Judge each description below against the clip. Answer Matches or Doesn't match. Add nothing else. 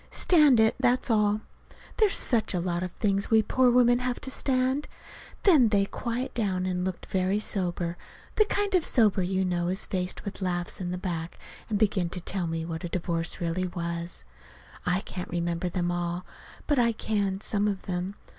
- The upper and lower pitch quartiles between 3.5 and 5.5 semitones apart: Matches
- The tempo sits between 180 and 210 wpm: Matches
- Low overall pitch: Doesn't match